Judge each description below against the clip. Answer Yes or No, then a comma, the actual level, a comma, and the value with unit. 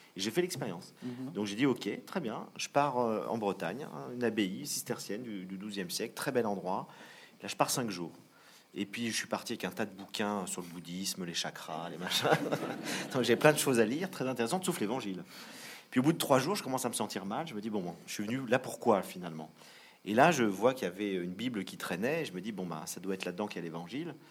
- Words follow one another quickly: Yes, fast, 255 wpm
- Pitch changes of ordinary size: Yes, average, 4.6 semitones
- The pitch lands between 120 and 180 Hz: No, low, 105 Hz